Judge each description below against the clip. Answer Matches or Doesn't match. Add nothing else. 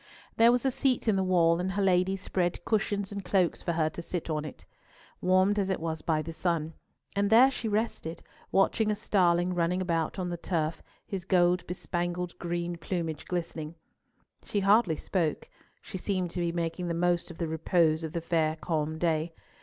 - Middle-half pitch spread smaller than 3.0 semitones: Matches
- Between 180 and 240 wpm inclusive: Matches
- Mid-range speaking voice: Matches